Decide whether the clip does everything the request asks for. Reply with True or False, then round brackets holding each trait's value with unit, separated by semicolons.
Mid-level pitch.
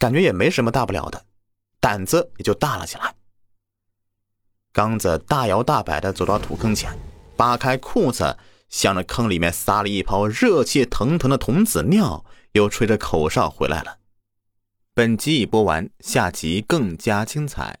False (100 Hz)